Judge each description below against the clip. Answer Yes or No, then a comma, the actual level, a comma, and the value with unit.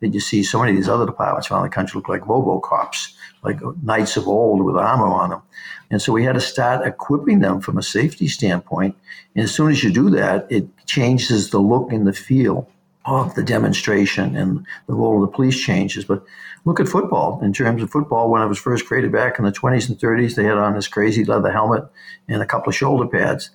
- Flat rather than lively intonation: No, average, 3.8 semitones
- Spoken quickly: Yes, fast, 235 wpm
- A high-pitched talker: No, low, 115 Hz